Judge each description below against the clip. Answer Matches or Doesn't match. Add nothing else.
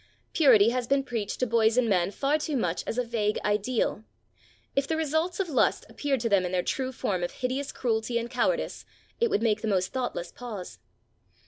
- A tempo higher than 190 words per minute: Matches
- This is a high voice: Matches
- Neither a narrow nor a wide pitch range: Matches